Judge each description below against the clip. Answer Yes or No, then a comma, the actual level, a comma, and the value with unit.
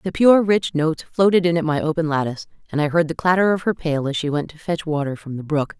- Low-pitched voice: No, medium, 160 Hz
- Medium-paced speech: No, fast, 280 wpm